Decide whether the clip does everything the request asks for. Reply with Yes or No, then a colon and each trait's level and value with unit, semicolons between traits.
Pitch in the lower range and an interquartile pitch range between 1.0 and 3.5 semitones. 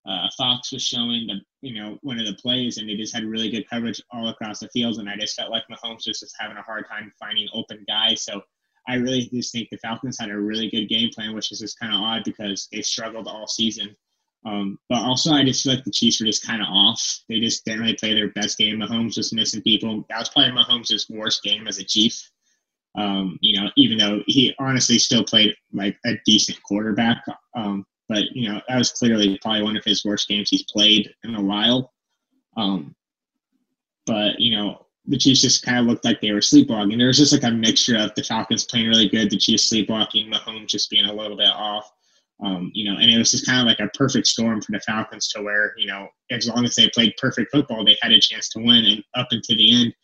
Yes: low, 110 Hz; narrow, 2.4 semitones